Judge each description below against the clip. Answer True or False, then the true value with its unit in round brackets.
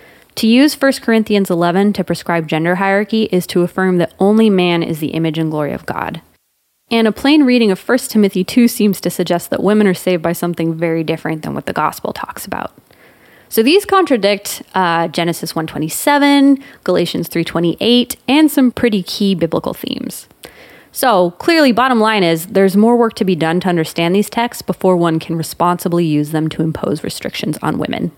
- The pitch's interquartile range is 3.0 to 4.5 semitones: False (5.4 semitones)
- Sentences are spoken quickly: False (185 wpm)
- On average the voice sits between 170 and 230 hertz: True (185 Hz)